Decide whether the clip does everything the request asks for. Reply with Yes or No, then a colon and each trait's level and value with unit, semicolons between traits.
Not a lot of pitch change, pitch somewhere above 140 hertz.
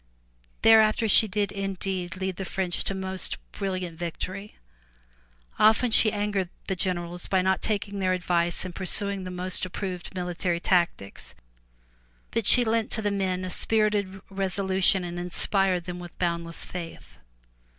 Yes: narrow, 2.0 semitones; high, 190 Hz